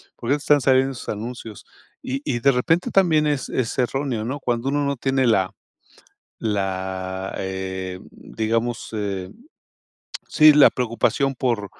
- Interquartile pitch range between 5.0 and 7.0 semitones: Yes, average, 5.3 semitones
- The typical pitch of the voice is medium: No, low, 120 Hz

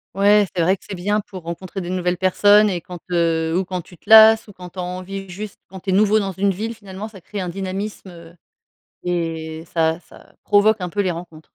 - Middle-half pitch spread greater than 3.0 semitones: No, average, 2.7 semitones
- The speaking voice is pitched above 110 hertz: Yes, medium, 185 Hz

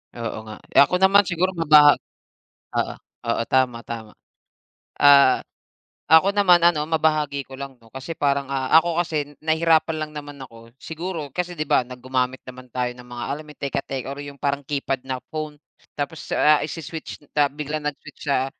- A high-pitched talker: No, medium, 145 Hz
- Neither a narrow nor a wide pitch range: Yes, average, 3.3 semitones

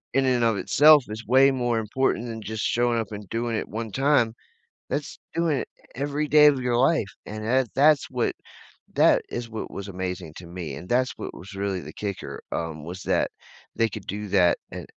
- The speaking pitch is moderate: No, low, 115 Hz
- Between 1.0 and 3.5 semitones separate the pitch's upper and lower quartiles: No, average, 4.8 semitones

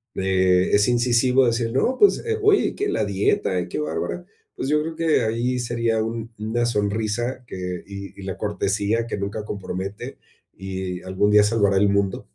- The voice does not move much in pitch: No, average, 3.6 semitones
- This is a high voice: No, low, 105 Hz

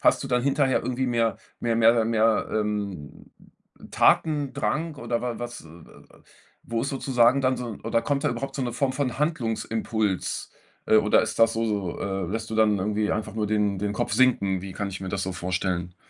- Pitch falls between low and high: No, low, 115 Hz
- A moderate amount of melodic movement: Yes, average, 3.9 semitones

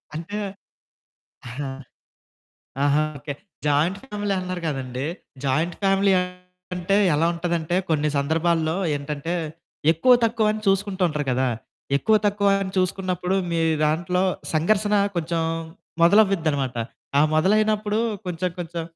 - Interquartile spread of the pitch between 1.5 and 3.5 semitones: No, average, 4.2 semitones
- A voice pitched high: No, medium, 175 Hz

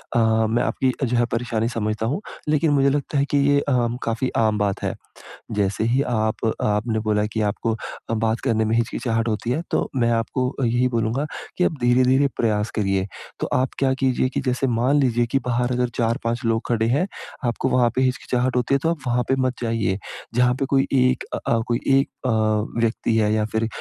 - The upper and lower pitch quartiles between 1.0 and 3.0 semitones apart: Yes, narrow, 2.5 semitones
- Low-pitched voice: Yes, low, 120 Hz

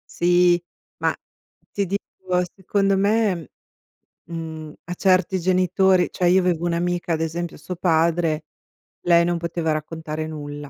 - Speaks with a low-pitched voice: No, medium, 175 Hz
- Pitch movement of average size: No, narrow, 2.2 semitones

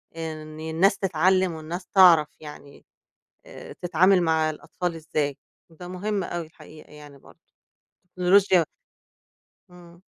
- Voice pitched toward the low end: No, medium, 170 Hz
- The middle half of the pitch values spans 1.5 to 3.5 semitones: Yes, average, 2.7 semitones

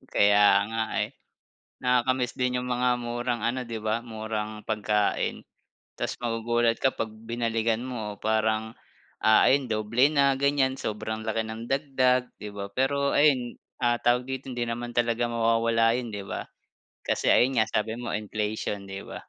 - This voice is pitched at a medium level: No, low, 115 Hz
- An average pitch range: No, narrow, 2.2 semitones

